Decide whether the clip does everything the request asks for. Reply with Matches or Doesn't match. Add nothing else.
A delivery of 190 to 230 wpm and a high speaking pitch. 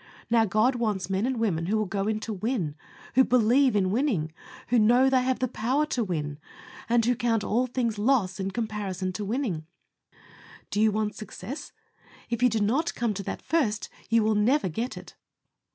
Matches